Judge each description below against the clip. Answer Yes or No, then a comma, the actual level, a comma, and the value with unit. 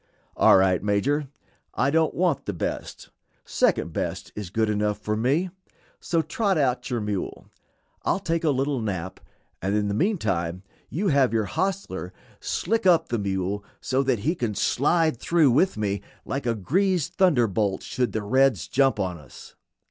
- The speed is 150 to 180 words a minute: Yes, average, 165 wpm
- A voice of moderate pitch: No, low, 125 Hz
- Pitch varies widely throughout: Yes, wide, 7.8 semitones